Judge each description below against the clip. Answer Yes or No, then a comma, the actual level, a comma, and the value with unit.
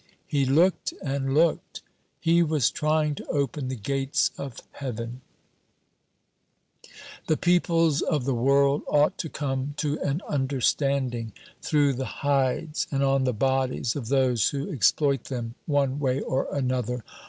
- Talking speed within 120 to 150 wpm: Yes, average, 140 wpm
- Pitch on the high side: No, medium, 140 Hz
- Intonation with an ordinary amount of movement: No, narrow, 2.2 semitones